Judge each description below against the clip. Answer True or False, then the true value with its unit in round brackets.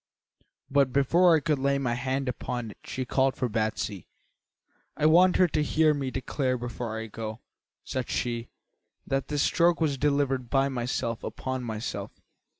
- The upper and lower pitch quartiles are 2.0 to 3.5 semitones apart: True (3.2 semitones)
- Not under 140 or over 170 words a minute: True (160 wpm)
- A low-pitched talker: True (130 Hz)